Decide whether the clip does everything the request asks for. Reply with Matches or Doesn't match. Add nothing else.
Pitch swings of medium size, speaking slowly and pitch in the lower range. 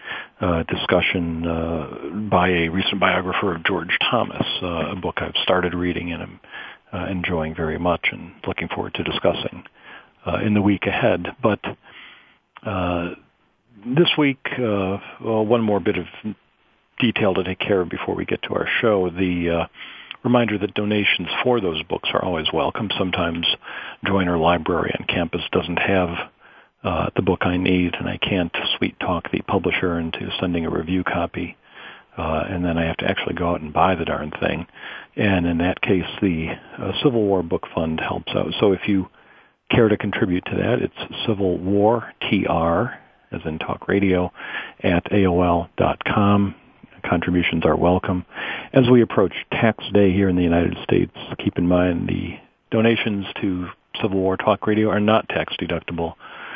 Doesn't match